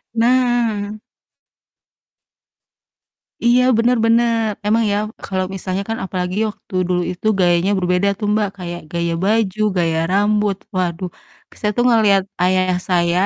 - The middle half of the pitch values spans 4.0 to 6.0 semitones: No, average, 3.6 semitones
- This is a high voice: Yes, high, 200 Hz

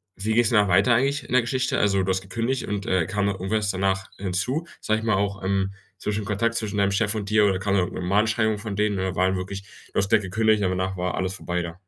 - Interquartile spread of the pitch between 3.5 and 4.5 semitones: No, narrow, 2.5 semitones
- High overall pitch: No, low, 100 Hz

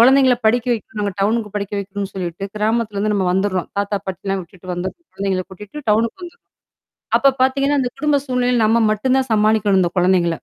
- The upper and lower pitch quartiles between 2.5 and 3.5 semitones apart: No, average, 4.2 semitones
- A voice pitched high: Yes, high, 210 Hz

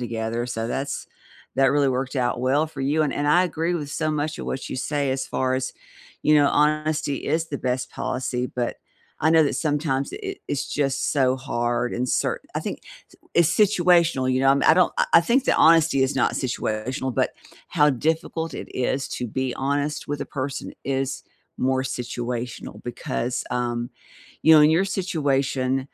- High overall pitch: No, low, 135 Hz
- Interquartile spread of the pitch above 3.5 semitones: No, average, 3.2 semitones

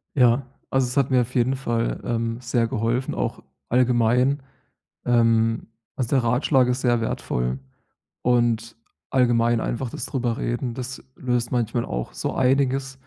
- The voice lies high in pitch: No, low, 120 Hz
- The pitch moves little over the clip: Yes, narrow, 1.8 semitones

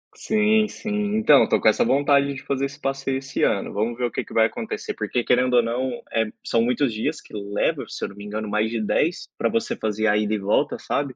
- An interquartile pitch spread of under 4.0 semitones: No, average, 4.5 semitones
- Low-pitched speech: Yes, low, 125 Hz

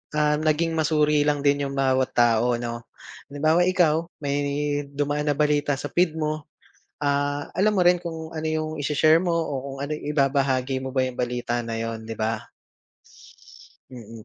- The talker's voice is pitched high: No, medium, 145 Hz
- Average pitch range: Yes, average, 3.0 semitones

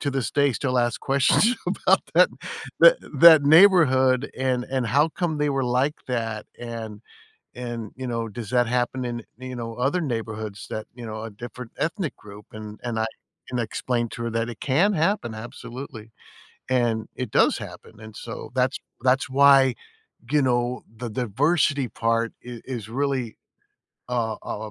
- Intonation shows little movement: No, average, 3.1 semitones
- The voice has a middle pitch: No, low, 125 Hz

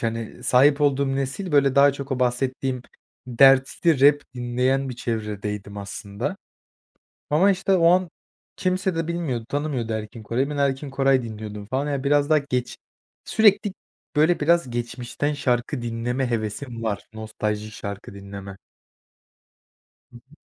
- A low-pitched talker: Yes, low, 130 Hz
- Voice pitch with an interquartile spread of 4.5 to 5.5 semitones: No, average, 4.1 semitones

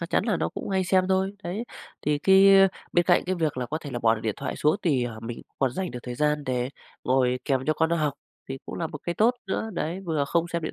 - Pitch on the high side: No, medium, 155 Hz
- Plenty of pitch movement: Yes, wide, 5.8 semitones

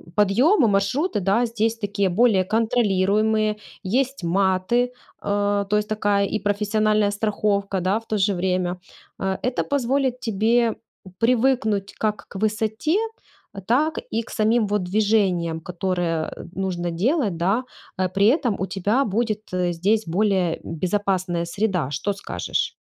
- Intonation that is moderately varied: Yes, average, 3.0 semitones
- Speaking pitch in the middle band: No, high, 205 Hz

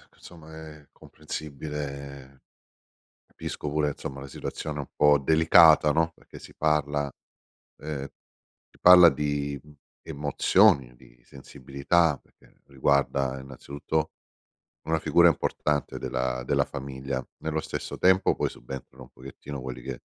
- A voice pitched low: Yes, very low, 70 Hz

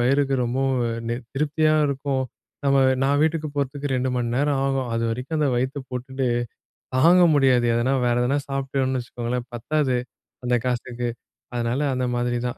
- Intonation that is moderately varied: No, narrow, 2.3 semitones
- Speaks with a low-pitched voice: Yes, low, 130 Hz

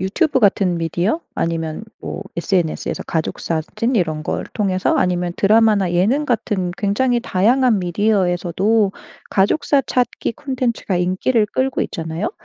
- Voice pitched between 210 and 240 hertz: No, high, 195 Hz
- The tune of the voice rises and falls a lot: No, average, 4.7 semitones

